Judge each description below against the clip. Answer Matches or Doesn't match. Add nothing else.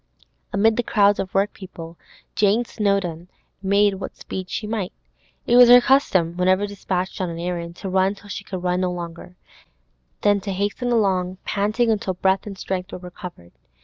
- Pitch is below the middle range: Doesn't match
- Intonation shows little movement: Matches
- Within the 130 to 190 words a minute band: Matches